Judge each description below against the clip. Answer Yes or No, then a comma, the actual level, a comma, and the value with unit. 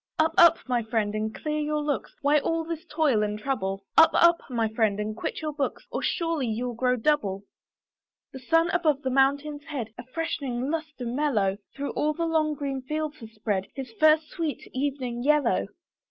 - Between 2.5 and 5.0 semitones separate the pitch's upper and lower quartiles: Yes, average, 4.7 semitones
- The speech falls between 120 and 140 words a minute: No, average, 185 wpm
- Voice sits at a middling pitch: No, very high, 275 Hz